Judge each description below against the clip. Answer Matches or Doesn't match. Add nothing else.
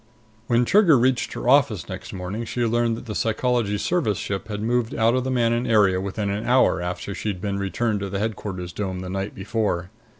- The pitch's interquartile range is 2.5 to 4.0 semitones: Matches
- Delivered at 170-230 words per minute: Matches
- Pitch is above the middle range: Doesn't match